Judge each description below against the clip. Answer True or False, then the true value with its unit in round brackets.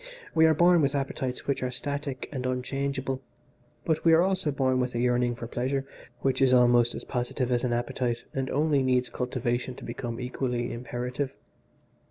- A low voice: True (130 Hz)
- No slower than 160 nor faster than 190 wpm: True (180 wpm)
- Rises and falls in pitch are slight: True (2.2 semitones)